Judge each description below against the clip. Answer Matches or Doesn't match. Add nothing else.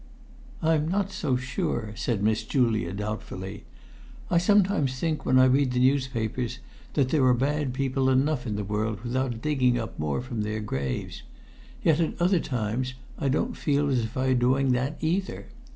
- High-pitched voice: Doesn't match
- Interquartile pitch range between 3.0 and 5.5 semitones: Matches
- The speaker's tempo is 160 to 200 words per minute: Matches